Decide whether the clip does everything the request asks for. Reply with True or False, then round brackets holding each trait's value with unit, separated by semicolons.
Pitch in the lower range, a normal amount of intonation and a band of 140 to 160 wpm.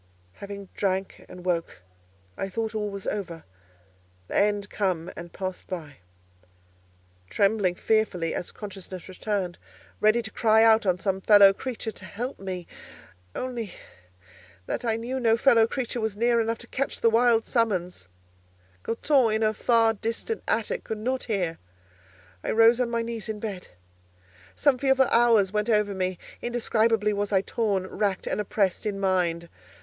False (210 Hz; 3.7 semitones; 145 wpm)